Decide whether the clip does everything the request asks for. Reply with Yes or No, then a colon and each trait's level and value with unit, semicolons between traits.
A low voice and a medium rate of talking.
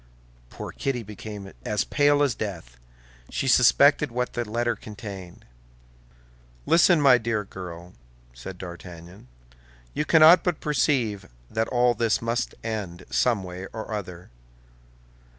No: low, 110 Hz; slow, 125 wpm